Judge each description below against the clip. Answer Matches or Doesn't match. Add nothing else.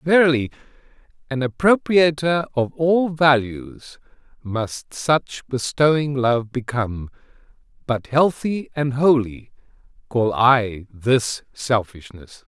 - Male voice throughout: Matches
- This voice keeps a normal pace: Doesn't match